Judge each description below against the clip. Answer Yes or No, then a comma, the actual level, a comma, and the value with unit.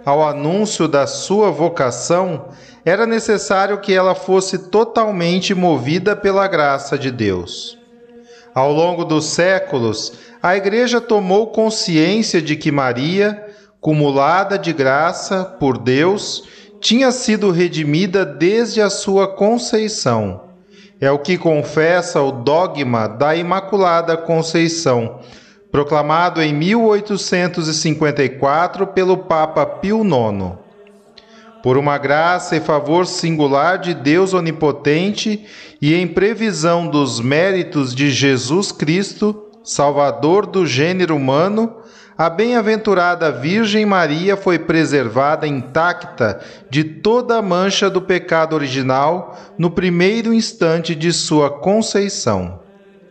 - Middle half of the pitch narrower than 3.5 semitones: No, average, 5.3 semitones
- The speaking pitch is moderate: Yes, medium, 175 Hz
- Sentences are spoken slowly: Yes, slow, 110 wpm